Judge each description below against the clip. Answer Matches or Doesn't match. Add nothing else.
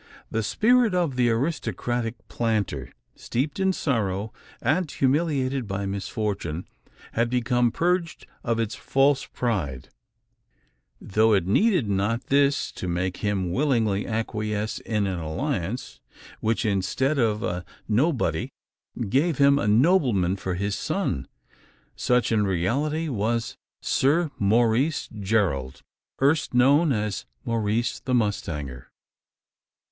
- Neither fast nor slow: Doesn't match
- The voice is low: Matches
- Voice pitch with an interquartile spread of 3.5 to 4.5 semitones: Doesn't match